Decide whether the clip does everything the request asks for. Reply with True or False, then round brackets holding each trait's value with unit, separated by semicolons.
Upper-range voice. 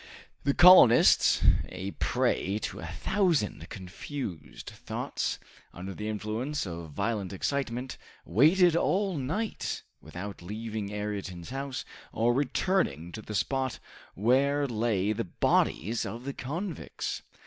False (115 Hz)